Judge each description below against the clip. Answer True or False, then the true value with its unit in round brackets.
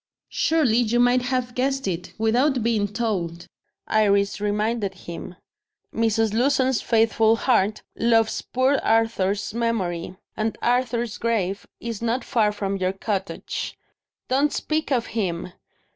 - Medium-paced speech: False (125 wpm)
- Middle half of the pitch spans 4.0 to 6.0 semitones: False (3.3 semitones)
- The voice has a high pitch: True (225 Hz)